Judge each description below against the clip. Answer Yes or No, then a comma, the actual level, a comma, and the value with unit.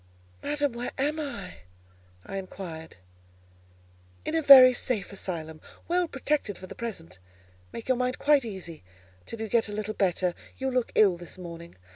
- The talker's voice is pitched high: Yes, high, 220 Hz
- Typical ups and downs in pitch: No, wide, 6.5 semitones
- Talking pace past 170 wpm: No, average, 160 wpm